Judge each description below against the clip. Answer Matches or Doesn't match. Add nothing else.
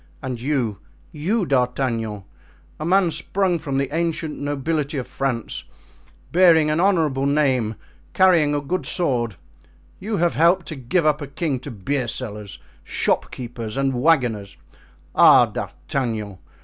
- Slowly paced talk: Matches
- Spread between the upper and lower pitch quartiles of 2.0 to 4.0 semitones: Doesn't match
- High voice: Doesn't match